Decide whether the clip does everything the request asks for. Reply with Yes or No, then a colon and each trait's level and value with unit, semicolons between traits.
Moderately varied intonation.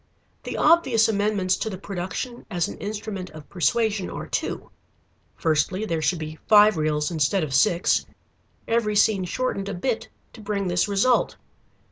Yes: average, 3.8 semitones